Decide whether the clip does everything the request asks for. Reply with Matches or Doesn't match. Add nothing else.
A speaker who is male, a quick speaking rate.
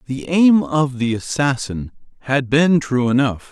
Doesn't match